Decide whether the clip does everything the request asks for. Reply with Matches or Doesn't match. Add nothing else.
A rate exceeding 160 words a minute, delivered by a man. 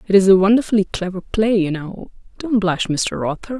Doesn't match